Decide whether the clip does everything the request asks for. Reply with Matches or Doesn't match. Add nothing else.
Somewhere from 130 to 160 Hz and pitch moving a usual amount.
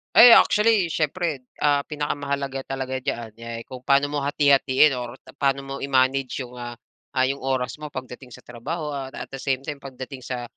Doesn't match